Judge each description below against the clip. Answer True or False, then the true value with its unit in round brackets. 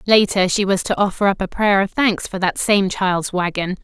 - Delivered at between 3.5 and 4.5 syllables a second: False (4.9 syllables/s)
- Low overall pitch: False (190 Hz)